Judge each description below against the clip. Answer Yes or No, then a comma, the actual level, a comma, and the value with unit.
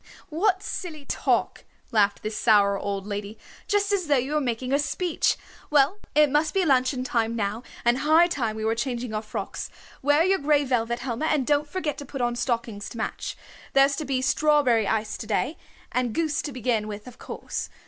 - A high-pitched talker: Yes, very high, 255 Hz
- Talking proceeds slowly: No, average, 200 wpm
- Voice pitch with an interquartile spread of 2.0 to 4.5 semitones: No, average, 5.0 semitones